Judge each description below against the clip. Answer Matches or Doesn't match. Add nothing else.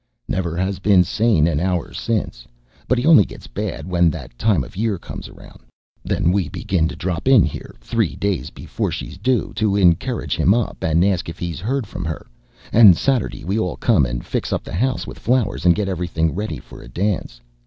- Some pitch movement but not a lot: Matches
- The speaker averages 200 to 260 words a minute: Matches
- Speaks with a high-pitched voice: Doesn't match